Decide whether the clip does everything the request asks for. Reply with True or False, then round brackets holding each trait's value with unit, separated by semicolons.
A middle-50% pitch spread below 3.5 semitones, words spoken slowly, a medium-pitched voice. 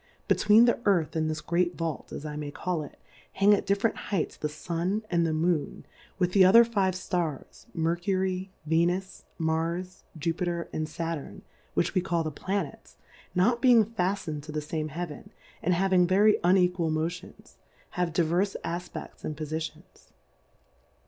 False (2.9 semitones; 155 wpm; 175 Hz)